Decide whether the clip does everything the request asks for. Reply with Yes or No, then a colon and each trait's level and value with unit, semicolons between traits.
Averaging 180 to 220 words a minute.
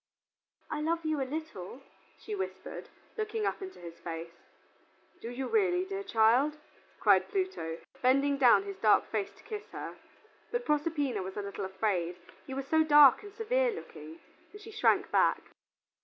No: average, 165 wpm